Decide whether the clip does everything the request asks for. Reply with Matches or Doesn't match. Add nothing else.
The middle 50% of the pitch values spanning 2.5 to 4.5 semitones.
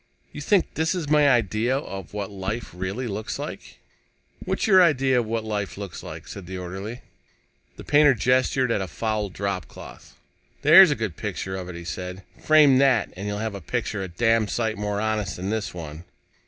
Doesn't match